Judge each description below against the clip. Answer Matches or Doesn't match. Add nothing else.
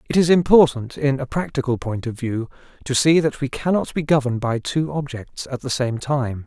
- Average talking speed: Doesn't match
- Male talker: Matches